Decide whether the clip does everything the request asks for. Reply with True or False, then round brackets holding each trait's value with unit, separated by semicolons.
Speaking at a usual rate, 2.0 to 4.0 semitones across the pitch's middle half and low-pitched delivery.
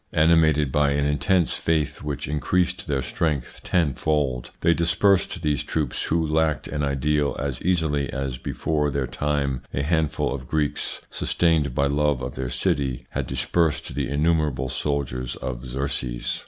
True (150 wpm; 2.7 semitones; 75 Hz)